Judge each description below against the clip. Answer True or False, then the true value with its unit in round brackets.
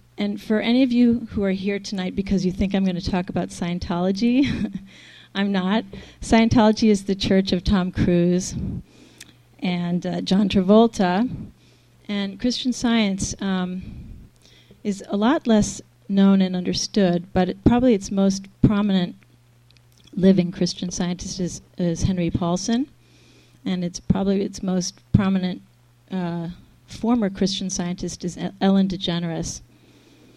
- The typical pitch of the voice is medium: False (195 Hz)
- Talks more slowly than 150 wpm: True (135 wpm)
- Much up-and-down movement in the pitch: False (2.6 semitones)